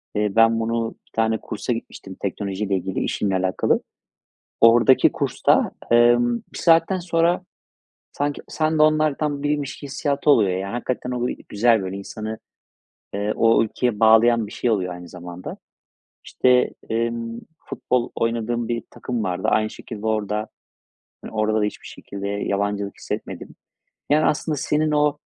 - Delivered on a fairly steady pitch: No, average, 3.7 semitones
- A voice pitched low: Yes, low, 115 Hz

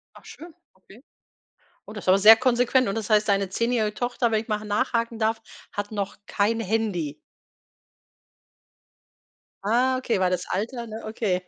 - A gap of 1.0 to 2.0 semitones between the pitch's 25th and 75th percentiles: No, narrow, 2.6 semitones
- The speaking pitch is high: Yes, high, 220 Hz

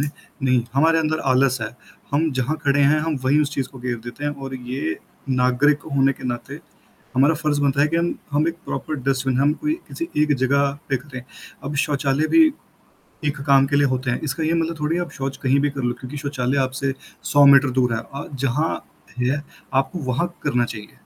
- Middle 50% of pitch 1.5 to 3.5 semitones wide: Yes, narrow, 2.5 semitones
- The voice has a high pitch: No, medium, 140 Hz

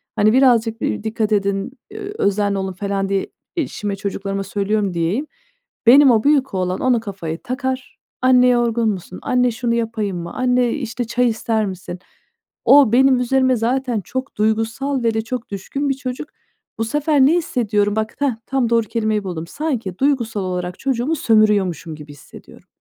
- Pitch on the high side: Yes, high, 225 Hz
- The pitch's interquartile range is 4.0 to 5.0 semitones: Yes, average, 4.4 semitones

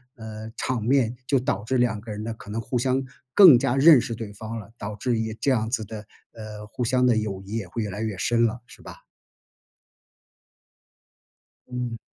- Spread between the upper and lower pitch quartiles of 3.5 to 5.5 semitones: No, narrow, 2.4 semitones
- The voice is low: Yes, low, 115 Hz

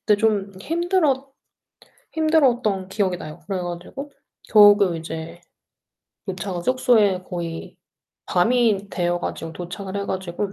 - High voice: Yes, high, 195 Hz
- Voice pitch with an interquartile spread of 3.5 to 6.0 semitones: Yes, average, 5.2 semitones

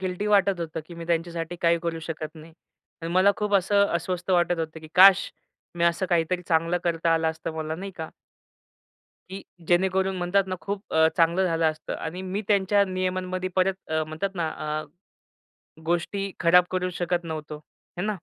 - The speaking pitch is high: No, medium, 175 Hz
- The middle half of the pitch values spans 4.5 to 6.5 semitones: No, narrow, 2.4 semitones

